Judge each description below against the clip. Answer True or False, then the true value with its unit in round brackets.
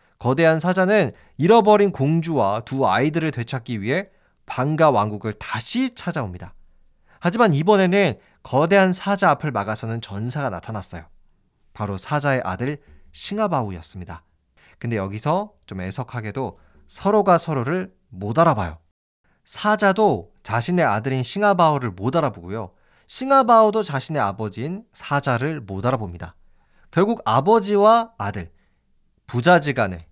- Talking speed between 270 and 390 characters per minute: True (305 characters per minute)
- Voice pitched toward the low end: True (130 Hz)